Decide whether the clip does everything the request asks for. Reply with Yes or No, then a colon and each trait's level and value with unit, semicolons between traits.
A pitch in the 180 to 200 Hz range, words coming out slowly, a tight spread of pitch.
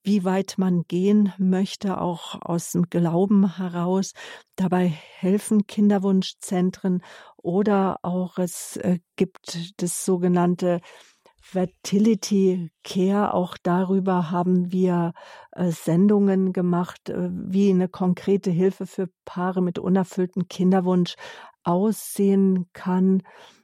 Yes: medium, 185 Hz; slow, 95 wpm; narrow, 1.4 semitones